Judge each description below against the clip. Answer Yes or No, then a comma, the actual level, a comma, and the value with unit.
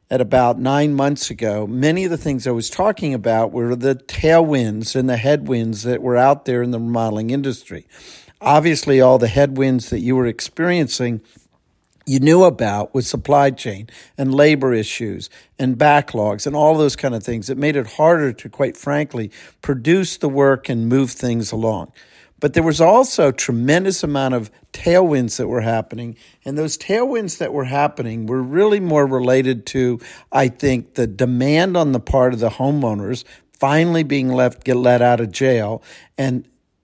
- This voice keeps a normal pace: Yes, average, 175 wpm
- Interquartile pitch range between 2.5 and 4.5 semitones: Yes, average, 3.4 semitones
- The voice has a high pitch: No, low, 130 Hz